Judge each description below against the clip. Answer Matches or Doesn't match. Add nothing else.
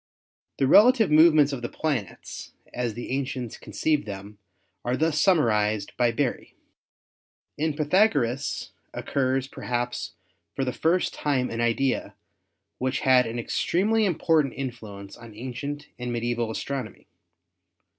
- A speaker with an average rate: Doesn't match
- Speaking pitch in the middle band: Doesn't match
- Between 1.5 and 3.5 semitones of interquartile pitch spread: Doesn't match